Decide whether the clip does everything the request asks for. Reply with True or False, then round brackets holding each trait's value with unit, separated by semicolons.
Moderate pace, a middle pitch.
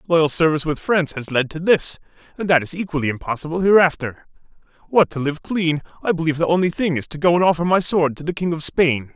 False (230 wpm; 160 Hz)